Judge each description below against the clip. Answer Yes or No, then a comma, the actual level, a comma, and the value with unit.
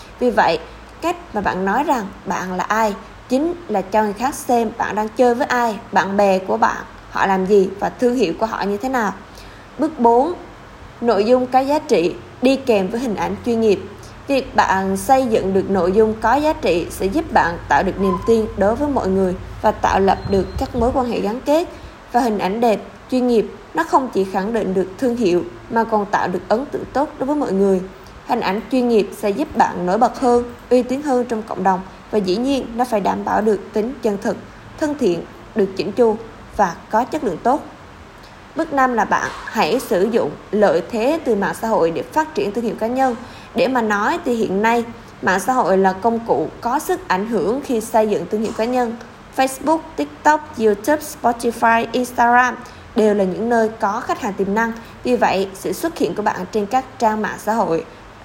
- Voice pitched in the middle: No, high, 225 Hz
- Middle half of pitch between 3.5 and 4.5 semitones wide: Yes, average, 4.0 semitones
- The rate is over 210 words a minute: Yes, average, 220 wpm